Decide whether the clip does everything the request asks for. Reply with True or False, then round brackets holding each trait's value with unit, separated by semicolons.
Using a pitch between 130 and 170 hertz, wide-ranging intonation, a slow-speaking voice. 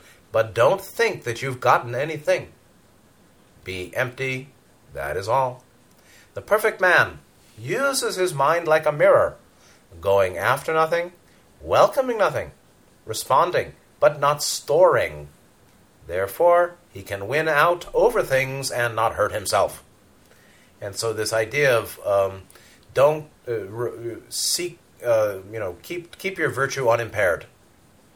True (135 Hz; 8.1 semitones; 125 wpm)